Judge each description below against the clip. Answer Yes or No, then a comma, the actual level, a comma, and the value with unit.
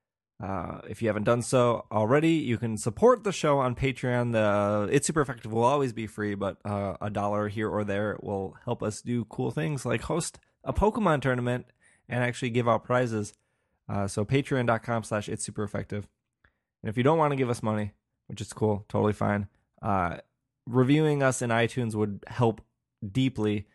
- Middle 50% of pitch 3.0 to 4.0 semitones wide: Yes, average, 3.6 semitones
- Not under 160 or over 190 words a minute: Yes, average, 185 wpm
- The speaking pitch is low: Yes, low, 115 Hz